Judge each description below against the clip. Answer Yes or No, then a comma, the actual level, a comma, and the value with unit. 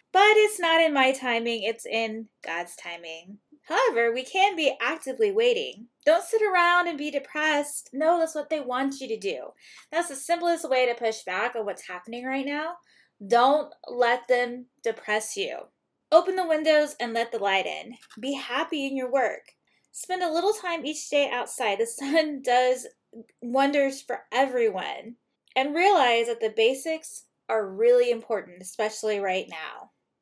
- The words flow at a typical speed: Yes, average, 165 wpm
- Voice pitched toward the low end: No, very high, 270 Hz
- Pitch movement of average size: No, wide, 5.9 semitones